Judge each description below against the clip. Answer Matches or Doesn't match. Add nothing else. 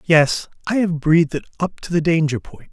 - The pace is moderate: Doesn't match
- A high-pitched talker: Doesn't match